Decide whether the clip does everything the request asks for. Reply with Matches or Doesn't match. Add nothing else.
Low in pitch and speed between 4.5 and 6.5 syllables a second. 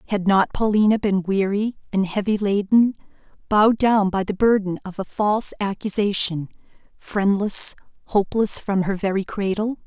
Doesn't match